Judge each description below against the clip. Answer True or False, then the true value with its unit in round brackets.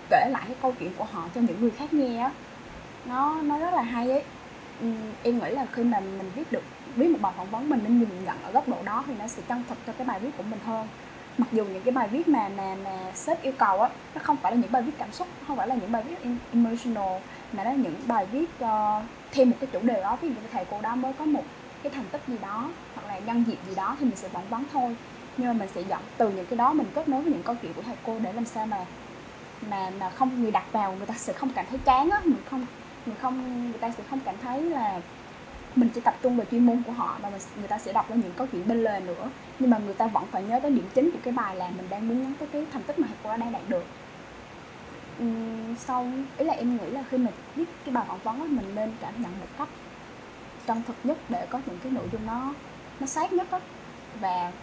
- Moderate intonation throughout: True (3.4 semitones)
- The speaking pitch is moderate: False (245 Hz)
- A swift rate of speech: True (275 wpm)